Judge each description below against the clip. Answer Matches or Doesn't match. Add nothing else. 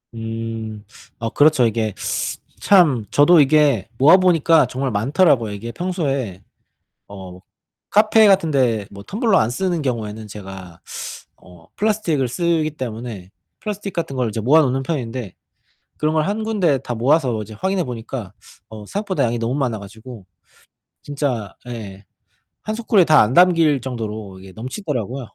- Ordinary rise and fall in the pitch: Doesn't match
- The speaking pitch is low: Matches